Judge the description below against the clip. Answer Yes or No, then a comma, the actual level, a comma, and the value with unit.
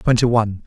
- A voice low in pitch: Yes, low, 115 Hz